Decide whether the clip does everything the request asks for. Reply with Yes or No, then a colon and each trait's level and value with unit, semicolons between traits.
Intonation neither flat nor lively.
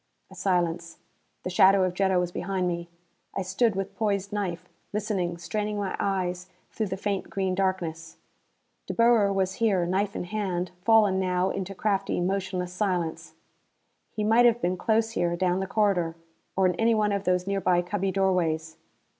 No: narrow, 2.2 semitones